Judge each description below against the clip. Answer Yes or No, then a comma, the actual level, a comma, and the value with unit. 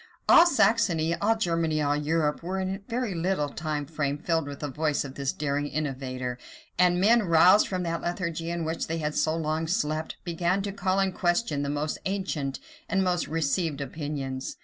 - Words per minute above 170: Yes, average, 185 wpm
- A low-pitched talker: No, medium, 165 Hz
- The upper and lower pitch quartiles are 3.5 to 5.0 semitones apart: Yes, average, 3.9 semitones